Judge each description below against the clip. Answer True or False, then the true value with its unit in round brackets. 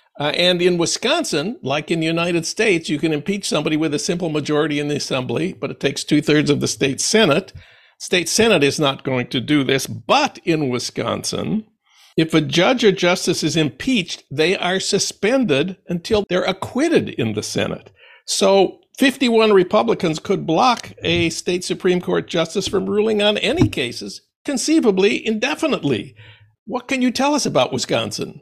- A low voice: False (180 Hz)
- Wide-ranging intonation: True (5.7 semitones)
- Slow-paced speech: False (170 wpm)